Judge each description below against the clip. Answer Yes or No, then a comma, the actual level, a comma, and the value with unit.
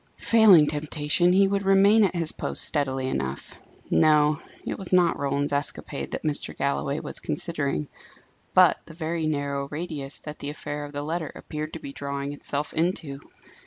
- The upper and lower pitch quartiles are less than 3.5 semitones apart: Yes, average, 3.1 semitones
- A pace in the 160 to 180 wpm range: Yes, average, 165 wpm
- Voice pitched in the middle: Yes, medium, 150 Hz